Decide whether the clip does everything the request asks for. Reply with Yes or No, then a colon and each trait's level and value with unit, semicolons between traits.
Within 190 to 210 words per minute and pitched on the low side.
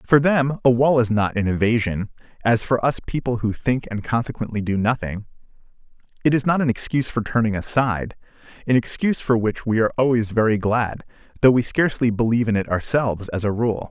Yes: average, 195 wpm; low, 115 Hz